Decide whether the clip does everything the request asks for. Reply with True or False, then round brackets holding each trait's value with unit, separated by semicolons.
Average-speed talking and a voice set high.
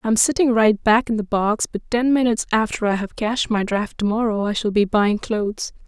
False (235 wpm; 220 Hz)